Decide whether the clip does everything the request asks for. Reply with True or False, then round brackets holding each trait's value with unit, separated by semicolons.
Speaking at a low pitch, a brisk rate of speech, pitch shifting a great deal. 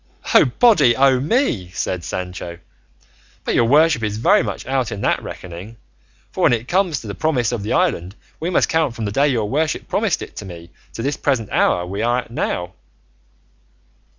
False (115 Hz; 195 wpm; 5.8 semitones)